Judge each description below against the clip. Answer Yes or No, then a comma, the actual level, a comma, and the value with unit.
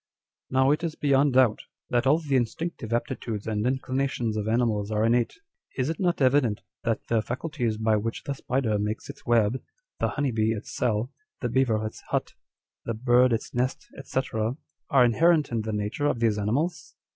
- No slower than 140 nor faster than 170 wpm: No, average, 185 wpm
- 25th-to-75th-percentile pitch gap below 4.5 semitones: Yes, average, 3.7 semitones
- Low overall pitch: Yes, low, 120 Hz